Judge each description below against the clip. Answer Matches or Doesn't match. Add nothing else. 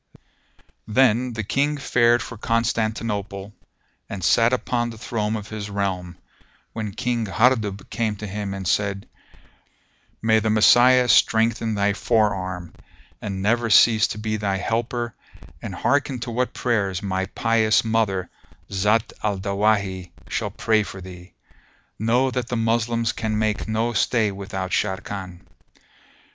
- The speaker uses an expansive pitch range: Doesn't match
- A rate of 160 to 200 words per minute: Doesn't match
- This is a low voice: Matches